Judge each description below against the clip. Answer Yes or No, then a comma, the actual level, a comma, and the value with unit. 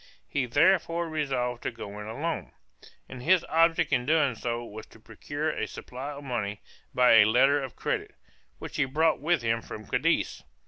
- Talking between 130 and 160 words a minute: No, average, 180 wpm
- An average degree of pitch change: Yes, average, 5.0 semitones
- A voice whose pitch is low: Yes, low, 130 Hz